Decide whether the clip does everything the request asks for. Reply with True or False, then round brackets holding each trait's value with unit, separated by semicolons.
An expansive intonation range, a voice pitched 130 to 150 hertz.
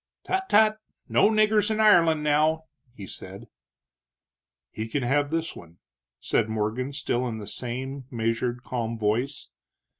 True (6.0 semitones; 135 Hz)